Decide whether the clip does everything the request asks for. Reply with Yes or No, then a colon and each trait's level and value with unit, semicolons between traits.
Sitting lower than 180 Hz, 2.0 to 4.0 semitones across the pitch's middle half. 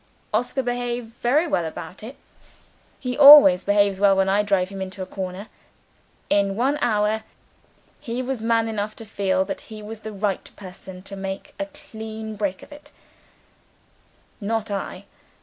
No: high, 210 Hz; average, 3.6 semitones